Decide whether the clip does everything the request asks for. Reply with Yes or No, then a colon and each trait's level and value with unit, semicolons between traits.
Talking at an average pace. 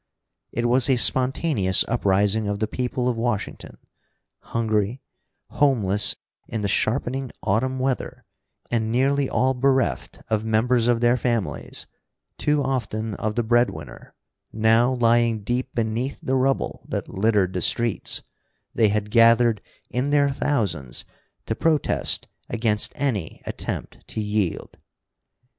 No: slow, 125 wpm